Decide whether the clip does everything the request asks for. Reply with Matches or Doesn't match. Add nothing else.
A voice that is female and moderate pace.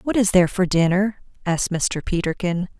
Matches